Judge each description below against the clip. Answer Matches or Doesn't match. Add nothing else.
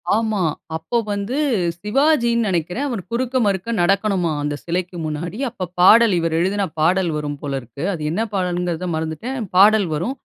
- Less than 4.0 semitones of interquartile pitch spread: Doesn't match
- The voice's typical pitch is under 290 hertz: Matches